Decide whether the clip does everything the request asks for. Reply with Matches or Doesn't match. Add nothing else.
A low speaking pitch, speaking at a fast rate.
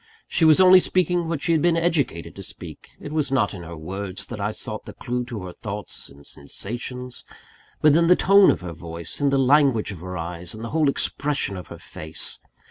Matches